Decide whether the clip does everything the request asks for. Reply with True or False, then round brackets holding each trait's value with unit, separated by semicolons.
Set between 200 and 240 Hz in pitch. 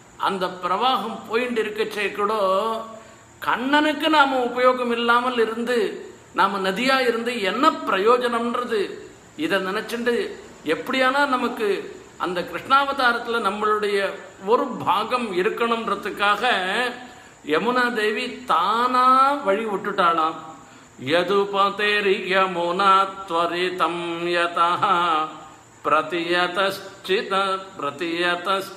True (215 Hz)